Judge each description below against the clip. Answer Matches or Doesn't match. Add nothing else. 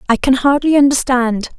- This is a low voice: Doesn't match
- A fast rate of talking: Doesn't match